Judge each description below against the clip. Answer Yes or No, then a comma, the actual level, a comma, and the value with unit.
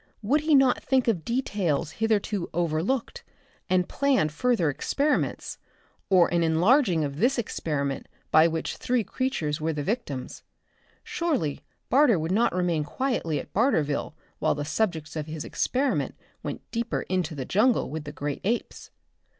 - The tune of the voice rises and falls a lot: Yes, wide, 7.9 semitones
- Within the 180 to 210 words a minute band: No, average, 150 wpm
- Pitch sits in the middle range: Yes, medium, 180 Hz